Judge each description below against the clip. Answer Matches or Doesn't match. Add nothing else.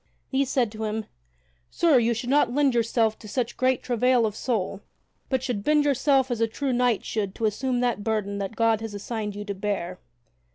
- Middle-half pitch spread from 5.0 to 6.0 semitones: Doesn't match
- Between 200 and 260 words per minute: Matches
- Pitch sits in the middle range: Doesn't match